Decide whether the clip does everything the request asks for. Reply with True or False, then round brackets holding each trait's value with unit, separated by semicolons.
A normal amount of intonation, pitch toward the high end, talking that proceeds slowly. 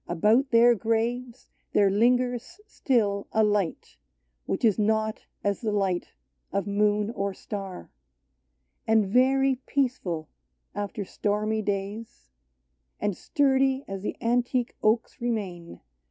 True (3.3 semitones; 215 Hz; 125 wpm)